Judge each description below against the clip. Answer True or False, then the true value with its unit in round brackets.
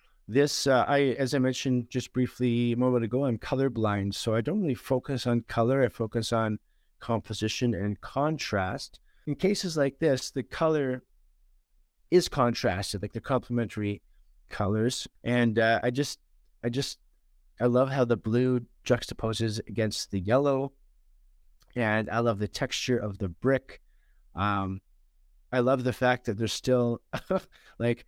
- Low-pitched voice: True (120 Hz)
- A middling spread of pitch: True (3.8 semitones)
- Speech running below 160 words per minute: True (150 wpm)